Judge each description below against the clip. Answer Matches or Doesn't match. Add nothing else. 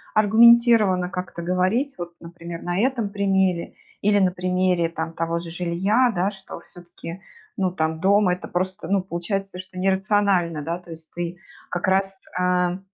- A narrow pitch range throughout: Matches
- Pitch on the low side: Doesn't match